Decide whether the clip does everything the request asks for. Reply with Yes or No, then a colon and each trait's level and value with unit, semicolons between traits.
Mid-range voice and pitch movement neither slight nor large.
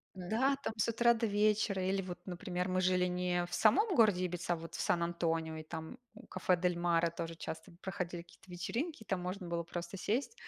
Yes: medium, 180 Hz; average, 3.4 semitones